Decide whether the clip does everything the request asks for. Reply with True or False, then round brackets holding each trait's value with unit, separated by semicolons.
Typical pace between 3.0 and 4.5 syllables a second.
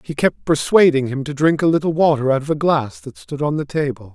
False (5.7 syllables/s)